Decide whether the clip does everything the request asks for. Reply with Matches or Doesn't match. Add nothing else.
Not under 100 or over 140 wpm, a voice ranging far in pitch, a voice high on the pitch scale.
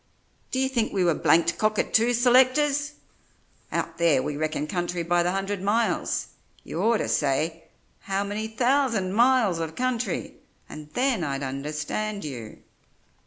Matches